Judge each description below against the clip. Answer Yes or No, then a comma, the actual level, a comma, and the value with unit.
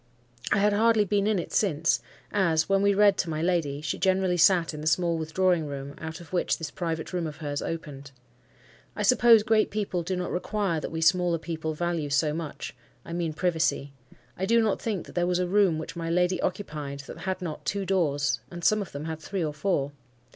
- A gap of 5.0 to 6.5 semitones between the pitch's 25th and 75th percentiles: No, average, 3.5 semitones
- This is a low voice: No, medium, 170 Hz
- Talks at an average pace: No, fast, 215 wpm